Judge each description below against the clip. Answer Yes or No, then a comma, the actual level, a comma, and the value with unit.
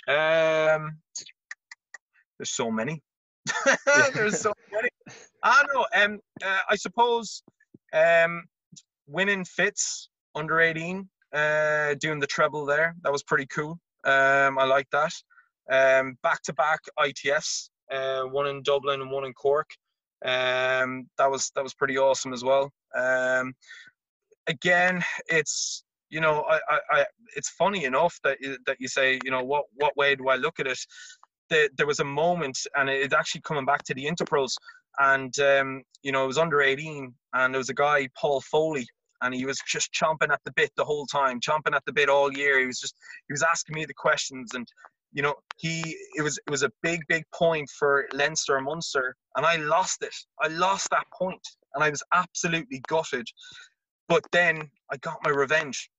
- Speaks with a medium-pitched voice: Yes, medium, 150 Hz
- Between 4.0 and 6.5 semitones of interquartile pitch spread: Yes, average, 5.1 semitones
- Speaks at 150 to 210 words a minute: Yes, average, 180 wpm